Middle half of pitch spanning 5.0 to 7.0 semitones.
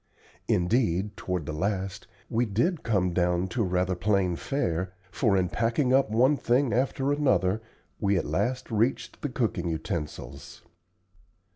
Yes: wide, 5.5 semitones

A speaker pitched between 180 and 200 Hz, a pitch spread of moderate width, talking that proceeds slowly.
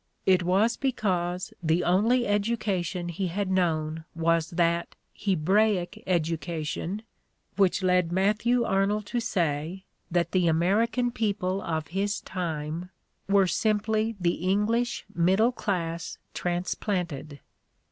Yes: medium, 185 Hz; average, 3.5 semitones; slow, 115 wpm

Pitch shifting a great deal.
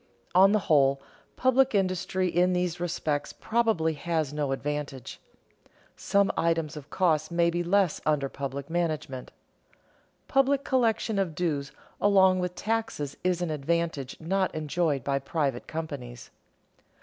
No: average, 4.3 semitones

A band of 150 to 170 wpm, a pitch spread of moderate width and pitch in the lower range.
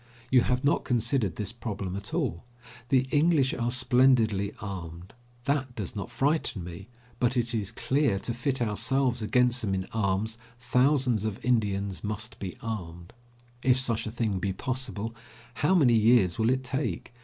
Yes: average, 165 wpm; average, 4.3 semitones; low, 115 Hz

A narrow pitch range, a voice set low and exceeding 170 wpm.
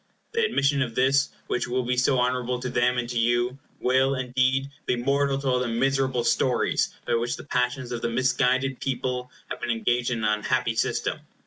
Yes: narrow, 1.6 semitones; low, 125 Hz; average, 200 wpm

